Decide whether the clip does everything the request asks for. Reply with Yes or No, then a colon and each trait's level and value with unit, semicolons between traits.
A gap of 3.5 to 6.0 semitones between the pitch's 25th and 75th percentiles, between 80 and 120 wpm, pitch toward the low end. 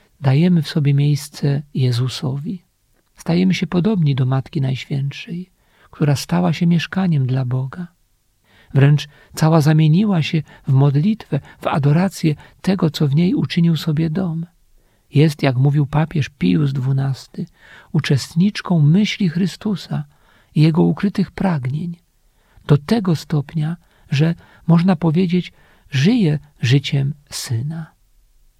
No: average, 3.9 semitones; average, 115 wpm; medium, 155 Hz